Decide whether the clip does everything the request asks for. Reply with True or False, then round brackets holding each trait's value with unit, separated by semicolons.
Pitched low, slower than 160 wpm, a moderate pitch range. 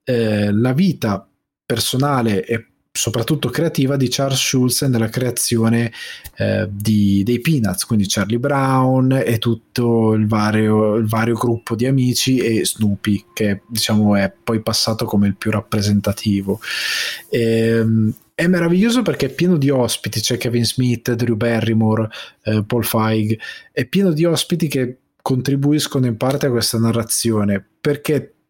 True (115 Hz; 145 wpm; 3.2 semitones)